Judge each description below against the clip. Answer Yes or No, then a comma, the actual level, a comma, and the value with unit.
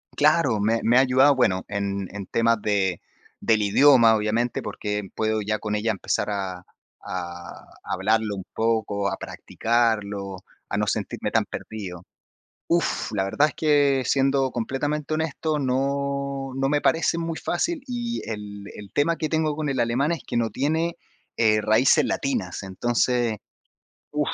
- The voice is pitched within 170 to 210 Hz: No, low, 115 Hz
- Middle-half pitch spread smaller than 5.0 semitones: No, wide, 5.4 semitones